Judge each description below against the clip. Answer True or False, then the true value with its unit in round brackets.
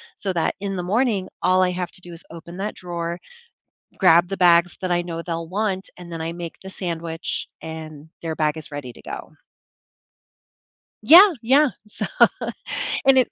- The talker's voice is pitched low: False (175 Hz)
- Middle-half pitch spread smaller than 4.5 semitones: True (2.5 semitones)